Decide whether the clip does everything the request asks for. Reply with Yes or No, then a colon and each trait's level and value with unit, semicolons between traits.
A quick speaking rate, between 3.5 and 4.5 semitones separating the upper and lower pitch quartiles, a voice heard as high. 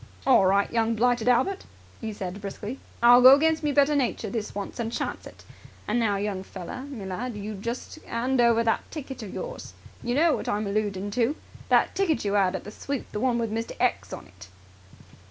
Yes: fast, 210 wpm; average, 4.0 semitones; high, 230 Hz